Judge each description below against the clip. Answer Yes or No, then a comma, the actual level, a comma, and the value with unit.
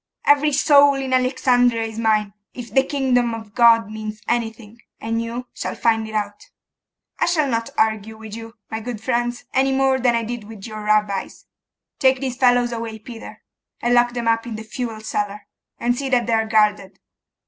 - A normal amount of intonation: No, narrow, 2.2 semitones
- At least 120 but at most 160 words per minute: No, average, 185 wpm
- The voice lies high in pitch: Yes, high, 230 Hz